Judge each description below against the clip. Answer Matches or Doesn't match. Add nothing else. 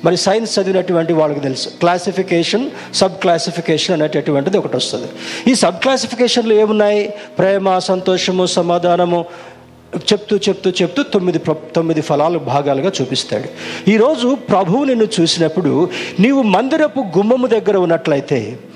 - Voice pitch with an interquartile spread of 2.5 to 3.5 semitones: Doesn't match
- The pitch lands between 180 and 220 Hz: Matches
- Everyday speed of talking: Matches